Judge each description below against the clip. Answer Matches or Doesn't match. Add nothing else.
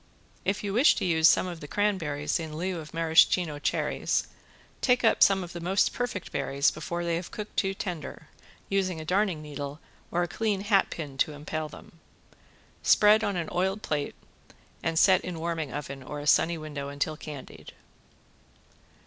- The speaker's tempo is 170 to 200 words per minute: Matches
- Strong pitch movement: Doesn't match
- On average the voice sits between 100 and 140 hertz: Doesn't match